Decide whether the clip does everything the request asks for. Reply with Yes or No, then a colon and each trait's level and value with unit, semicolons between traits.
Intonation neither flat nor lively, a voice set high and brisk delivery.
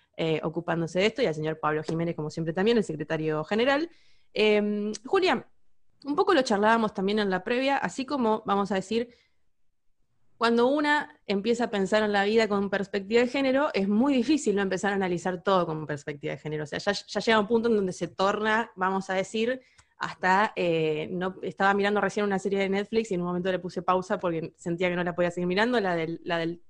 Yes: average, 4.1 semitones; high, 200 Hz; fast, 220 wpm